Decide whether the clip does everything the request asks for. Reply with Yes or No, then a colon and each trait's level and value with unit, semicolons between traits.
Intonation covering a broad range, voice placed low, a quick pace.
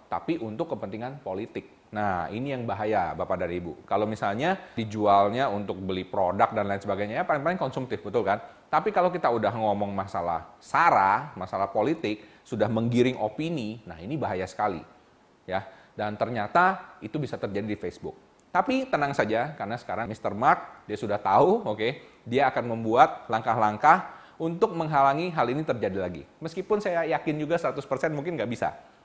Yes: wide, 7.1 semitones; low, 115 Hz; fast, 165 wpm